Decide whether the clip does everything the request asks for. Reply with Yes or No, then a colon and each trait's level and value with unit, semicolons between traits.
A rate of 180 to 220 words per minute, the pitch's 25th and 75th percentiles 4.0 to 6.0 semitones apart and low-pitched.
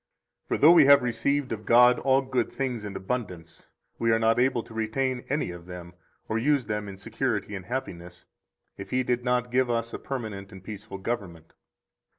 Yes: average, 190 wpm; average, 4.6 semitones; low, 115 Hz